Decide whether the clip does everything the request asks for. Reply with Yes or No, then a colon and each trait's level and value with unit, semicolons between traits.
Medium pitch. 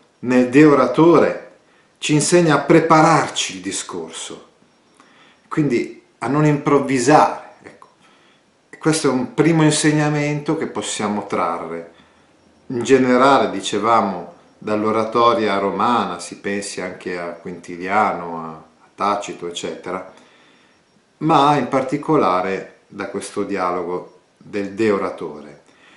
No: low, 125 Hz